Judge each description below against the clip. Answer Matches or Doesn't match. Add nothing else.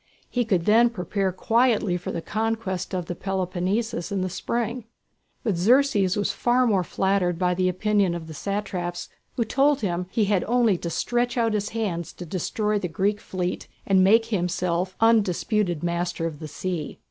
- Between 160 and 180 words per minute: Matches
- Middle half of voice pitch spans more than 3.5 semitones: Matches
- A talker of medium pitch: Doesn't match